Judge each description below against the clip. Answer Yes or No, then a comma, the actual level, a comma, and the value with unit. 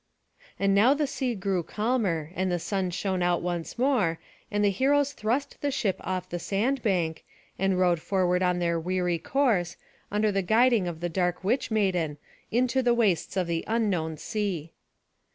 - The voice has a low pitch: No, high, 190 Hz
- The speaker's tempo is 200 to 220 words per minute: No, average, 175 wpm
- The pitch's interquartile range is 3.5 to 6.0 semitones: Yes, average, 4.5 semitones